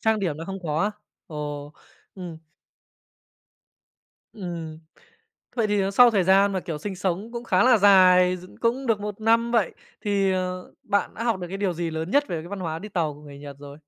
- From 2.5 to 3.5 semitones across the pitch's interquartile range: No, average, 4.0 semitones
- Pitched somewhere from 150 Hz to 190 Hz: Yes, medium, 185 Hz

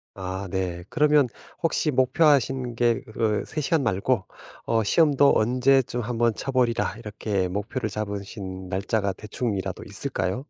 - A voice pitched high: No, low, 115 Hz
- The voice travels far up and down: No, average, 4.7 semitones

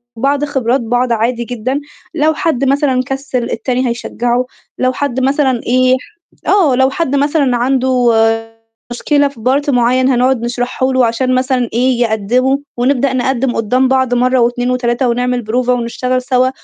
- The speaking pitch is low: No, very high, 255 Hz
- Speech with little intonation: Yes, narrow, 1.6 semitones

